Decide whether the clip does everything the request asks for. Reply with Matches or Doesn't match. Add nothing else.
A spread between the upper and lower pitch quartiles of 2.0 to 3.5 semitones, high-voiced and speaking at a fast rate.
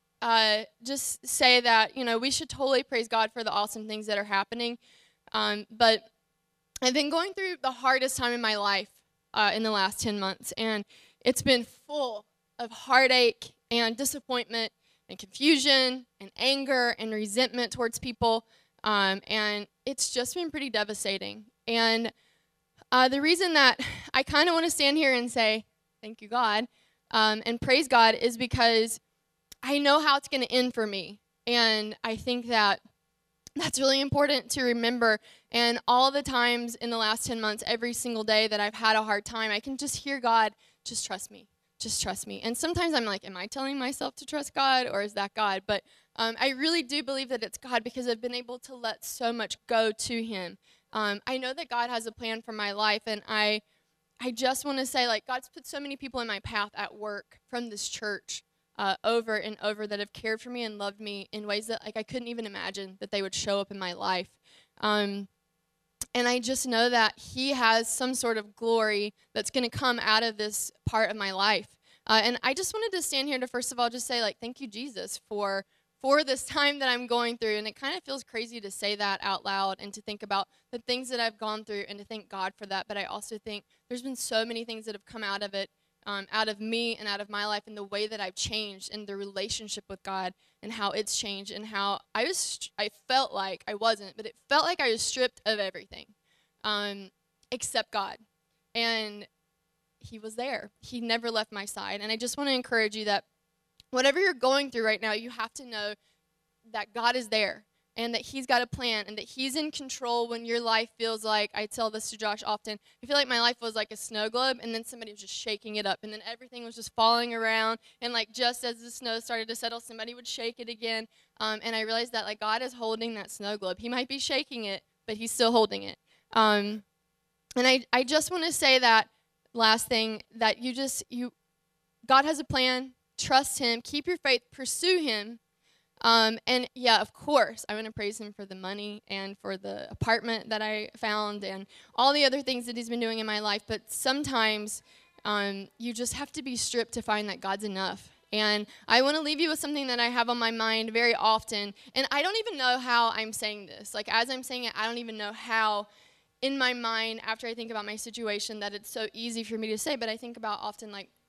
Matches